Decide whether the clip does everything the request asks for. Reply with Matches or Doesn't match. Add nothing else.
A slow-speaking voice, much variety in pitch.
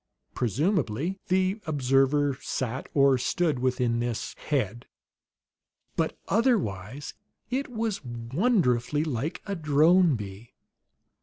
Matches